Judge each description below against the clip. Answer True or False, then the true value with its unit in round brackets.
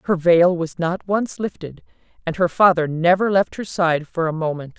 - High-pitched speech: False (175 Hz)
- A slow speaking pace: False (200 wpm)